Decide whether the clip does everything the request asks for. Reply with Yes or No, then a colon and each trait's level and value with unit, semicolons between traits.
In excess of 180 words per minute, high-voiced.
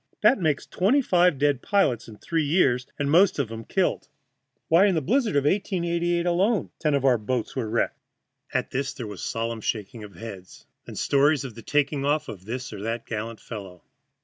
No: average, 200 wpm; medium, 140 Hz